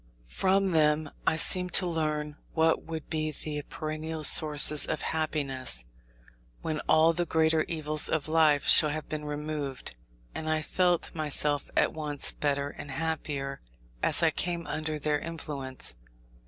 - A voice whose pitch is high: No, medium, 155 Hz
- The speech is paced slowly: No, average, 145 wpm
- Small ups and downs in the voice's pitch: Yes, narrow, 1.4 semitones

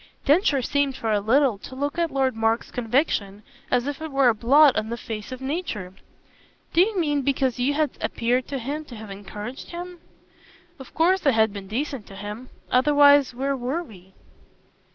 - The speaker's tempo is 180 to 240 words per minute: Yes, average, 190 wpm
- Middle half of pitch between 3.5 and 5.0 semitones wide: Yes, average, 4.5 semitones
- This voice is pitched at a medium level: No, very high, 260 Hz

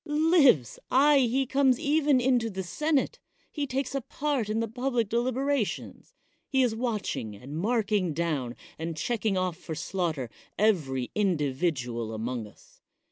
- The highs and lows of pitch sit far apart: Yes, wide, 8.8 semitones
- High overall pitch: Yes, high, 220 Hz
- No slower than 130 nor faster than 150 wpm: Yes, average, 140 wpm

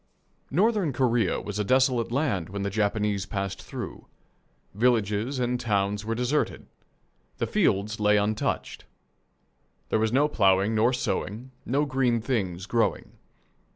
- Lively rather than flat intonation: No, average, 3.8 semitones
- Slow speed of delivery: Yes, slow, 130 wpm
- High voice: No, low, 110 Hz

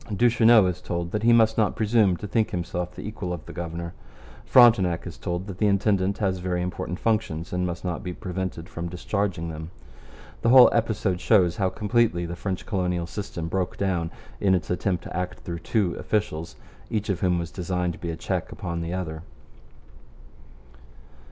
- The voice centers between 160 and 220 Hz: No, very low, 90 Hz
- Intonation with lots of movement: No, average, 3.3 semitones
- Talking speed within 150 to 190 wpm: Yes, average, 185 wpm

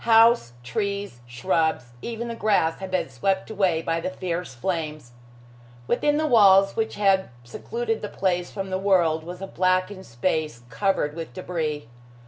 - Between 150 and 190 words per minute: Yes, average, 155 wpm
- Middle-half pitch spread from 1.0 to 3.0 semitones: No, average, 4.1 semitones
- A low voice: No, medium, 185 Hz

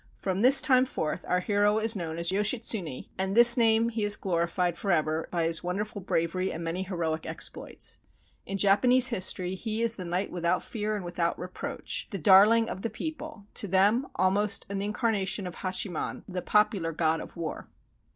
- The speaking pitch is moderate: No, high, 195 Hz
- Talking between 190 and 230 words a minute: No, average, 180 wpm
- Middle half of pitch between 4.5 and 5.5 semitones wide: No, average, 3.9 semitones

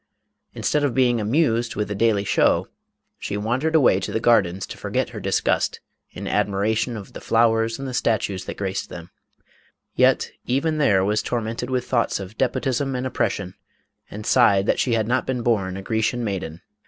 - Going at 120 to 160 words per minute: No, average, 180 wpm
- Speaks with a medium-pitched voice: No, low, 115 Hz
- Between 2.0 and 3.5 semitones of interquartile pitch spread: No, average, 3.9 semitones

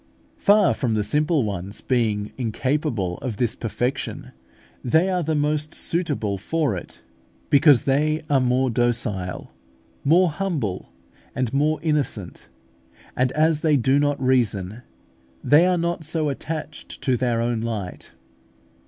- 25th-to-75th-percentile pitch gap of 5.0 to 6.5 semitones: Yes, average, 5.3 semitones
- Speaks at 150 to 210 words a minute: No, slow, 135 wpm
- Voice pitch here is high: No, low, 130 Hz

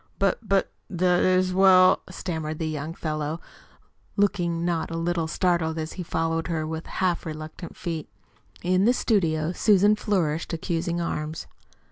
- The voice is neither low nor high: Yes, medium, 170 Hz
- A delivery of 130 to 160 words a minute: Yes, average, 150 wpm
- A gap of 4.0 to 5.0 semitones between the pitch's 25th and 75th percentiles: No, narrow, 2.4 semitones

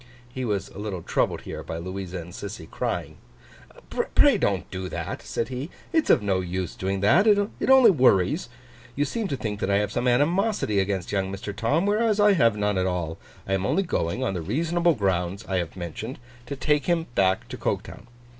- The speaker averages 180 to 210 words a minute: Yes, average, 200 wpm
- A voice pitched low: Yes, low, 105 Hz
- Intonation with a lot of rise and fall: Yes, wide, 8.0 semitones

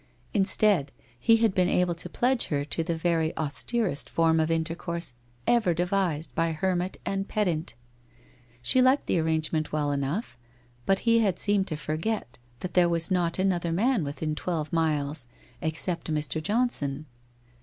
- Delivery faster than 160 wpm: No, average, 155 wpm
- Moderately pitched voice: Yes, medium, 170 Hz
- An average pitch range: Yes, average, 3.8 semitones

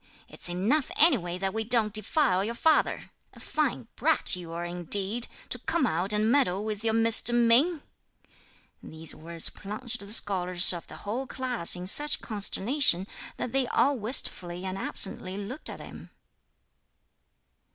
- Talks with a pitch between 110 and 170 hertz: No, high, 210 Hz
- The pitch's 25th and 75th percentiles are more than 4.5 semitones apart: Yes, average, 5.3 semitones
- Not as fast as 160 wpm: Yes, average, 150 wpm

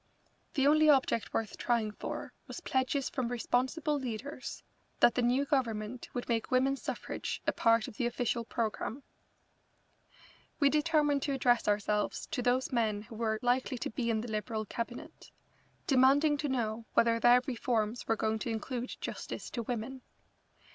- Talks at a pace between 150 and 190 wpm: Yes, average, 160 wpm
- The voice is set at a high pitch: Yes, high, 245 Hz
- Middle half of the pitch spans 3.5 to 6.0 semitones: No, average, 2.9 semitones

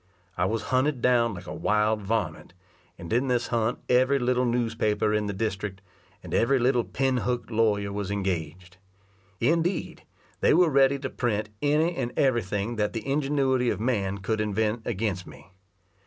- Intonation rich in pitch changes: No, average, 3.8 semitones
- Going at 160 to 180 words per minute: Yes, average, 170 wpm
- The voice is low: Yes, low, 115 Hz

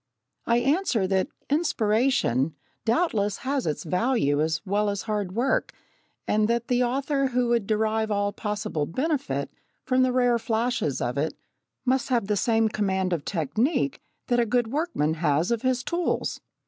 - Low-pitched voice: No, high, 220 Hz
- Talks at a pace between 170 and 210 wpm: No, average, 160 wpm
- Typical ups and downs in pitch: Yes, average, 5.0 semitones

